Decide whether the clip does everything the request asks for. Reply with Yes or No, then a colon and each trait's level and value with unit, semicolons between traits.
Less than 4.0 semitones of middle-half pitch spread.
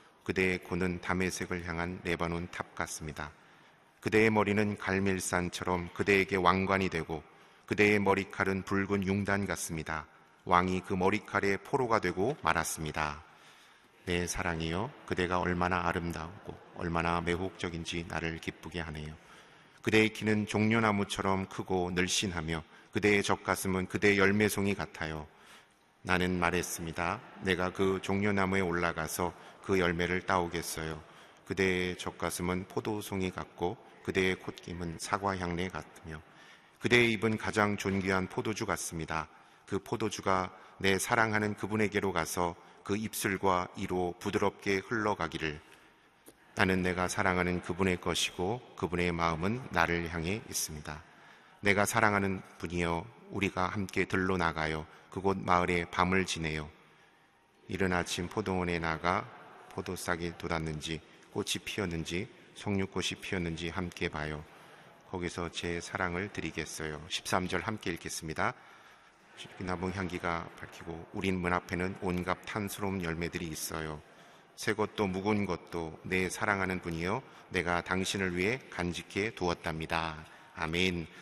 Yes: narrow, 2.5 semitones